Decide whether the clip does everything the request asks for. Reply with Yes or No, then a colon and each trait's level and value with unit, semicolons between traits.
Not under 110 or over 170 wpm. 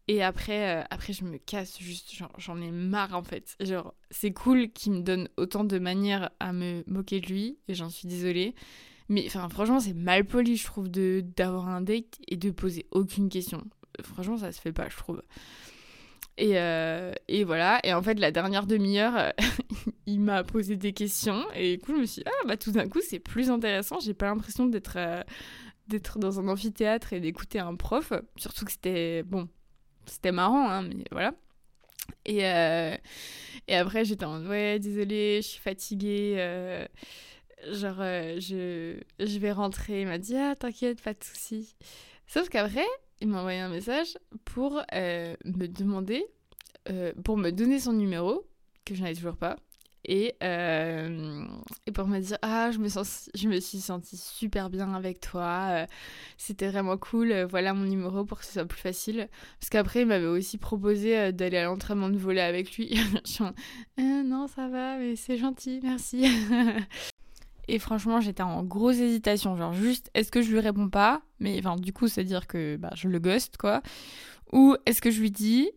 No: average, 190 wpm